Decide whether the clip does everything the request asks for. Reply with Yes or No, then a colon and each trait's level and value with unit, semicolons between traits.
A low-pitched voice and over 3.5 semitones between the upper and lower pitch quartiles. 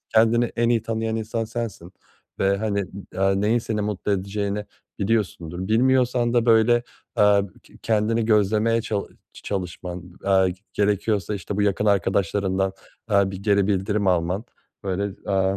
No: low, 105 Hz; narrow, 2.5 semitones